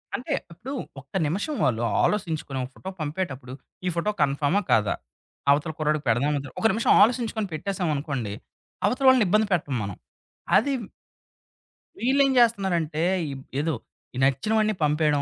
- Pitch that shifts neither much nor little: No, wide, 7.1 semitones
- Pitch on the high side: No, medium, 160 Hz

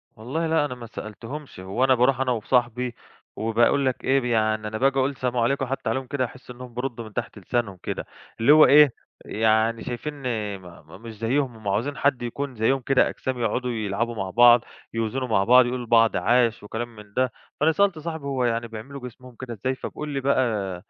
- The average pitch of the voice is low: Yes, low, 120 Hz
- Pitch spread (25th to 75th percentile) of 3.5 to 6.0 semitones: No, average, 3.1 semitones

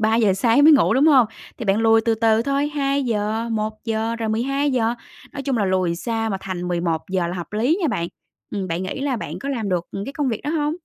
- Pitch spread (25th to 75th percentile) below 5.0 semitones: No, wide, 5.6 semitones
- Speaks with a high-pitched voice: Yes, high, 225 Hz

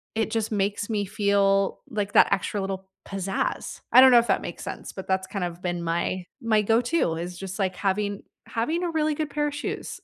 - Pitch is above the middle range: Yes, high, 200 Hz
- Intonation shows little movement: No, average, 3.3 semitones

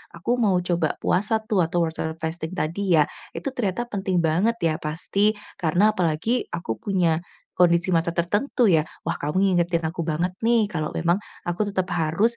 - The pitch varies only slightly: No, average, 3.2 semitones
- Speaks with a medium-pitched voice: Yes, medium, 175 Hz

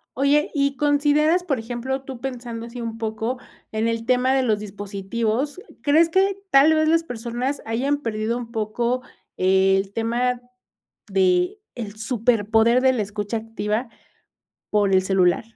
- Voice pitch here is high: Yes, high, 235 Hz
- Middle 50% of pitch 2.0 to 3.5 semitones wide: No, average, 4.0 semitones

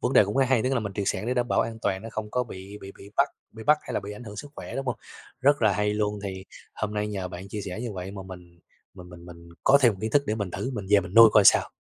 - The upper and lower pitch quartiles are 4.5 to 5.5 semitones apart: No, average, 3.3 semitones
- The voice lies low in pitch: Yes, low, 105 Hz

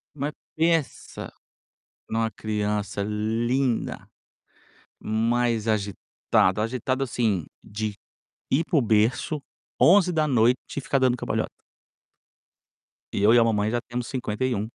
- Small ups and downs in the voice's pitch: No, average, 3.4 semitones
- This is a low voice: Yes, low, 115 Hz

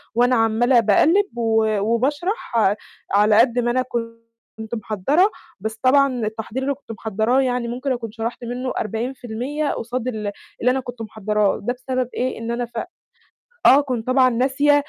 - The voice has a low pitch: No, high, 240 Hz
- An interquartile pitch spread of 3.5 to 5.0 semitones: No, average, 2.8 semitones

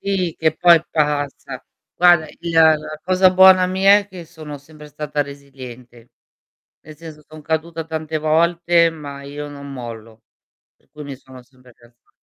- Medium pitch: Yes, medium, 155 Hz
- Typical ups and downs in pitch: Yes, average, 3.1 semitones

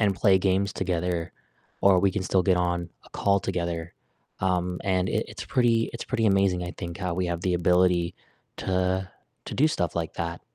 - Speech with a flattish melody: Yes, narrow, 1.9 semitones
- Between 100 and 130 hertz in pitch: No, very low, 90 Hz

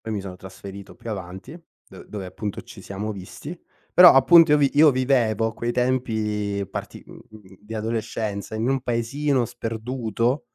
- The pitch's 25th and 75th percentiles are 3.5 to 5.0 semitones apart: Yes, average, 3.8 semitones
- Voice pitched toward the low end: Yes, low, 115 Hz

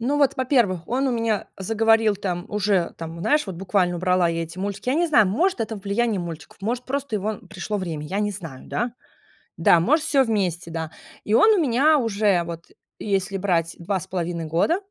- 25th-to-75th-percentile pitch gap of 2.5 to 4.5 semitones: No, average, 5.2 semitones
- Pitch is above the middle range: Yes, high, 200 Hz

